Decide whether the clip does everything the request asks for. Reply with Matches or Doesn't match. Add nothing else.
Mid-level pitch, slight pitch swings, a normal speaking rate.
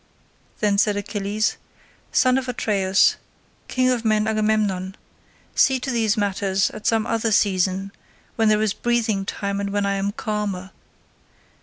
Doesn't match